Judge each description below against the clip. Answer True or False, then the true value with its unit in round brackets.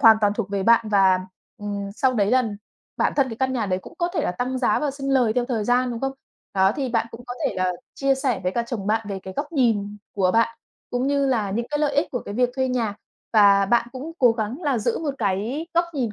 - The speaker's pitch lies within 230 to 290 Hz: True (235 Hz)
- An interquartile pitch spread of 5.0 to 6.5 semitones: False (4.3 semitones)